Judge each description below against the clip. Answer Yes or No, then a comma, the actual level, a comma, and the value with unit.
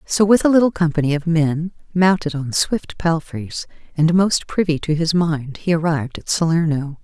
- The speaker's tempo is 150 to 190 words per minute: Yes, average, 180 wpm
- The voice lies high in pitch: No, medium, 165 Hz